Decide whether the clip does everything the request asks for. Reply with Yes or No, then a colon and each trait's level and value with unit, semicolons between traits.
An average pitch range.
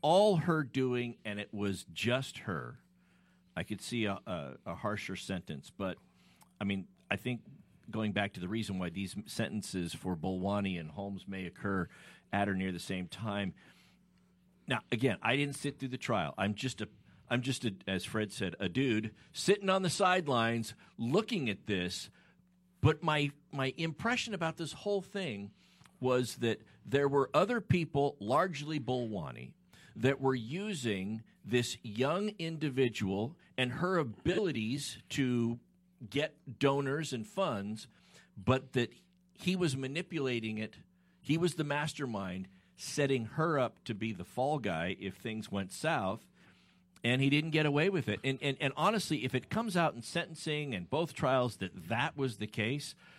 No: wide, 6.8 semitones